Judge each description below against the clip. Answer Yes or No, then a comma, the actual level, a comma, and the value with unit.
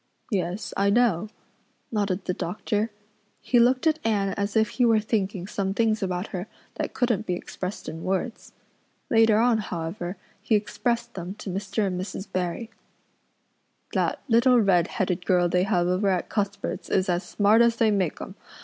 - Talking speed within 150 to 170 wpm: Yes, average, 165 wpm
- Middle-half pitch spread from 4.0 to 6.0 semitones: No, average, 3.5 semitones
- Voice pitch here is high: Yes, high, 200 Hz